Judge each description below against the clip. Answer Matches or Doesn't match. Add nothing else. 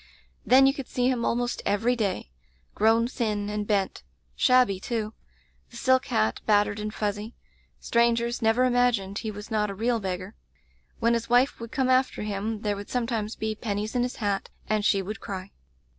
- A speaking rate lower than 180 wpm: Doesn't match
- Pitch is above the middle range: Matches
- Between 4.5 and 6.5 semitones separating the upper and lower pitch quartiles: Doesn't match